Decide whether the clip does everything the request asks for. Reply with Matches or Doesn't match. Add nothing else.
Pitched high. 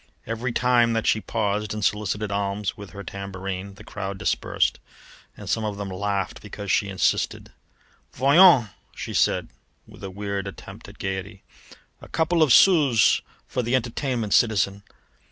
Doesn't match